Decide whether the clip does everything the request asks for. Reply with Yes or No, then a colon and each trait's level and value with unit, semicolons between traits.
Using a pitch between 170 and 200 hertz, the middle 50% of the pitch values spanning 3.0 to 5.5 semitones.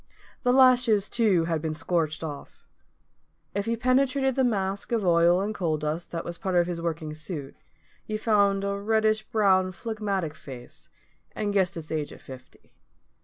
Yes: high, 190 Hz; average, 4.8 semitones